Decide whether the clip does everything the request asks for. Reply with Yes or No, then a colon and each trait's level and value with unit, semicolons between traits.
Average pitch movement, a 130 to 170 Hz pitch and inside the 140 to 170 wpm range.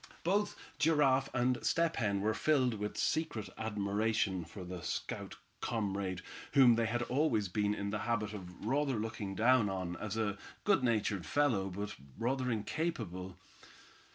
No: average, 4.4 semitones; low, 110 Hz; average, 150 wpm